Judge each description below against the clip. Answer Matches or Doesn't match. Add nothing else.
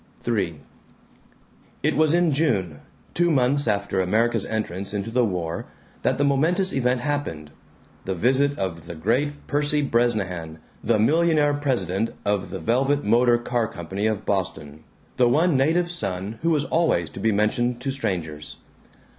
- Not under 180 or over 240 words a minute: Doesn't match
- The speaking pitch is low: Matches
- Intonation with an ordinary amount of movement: Doesn't match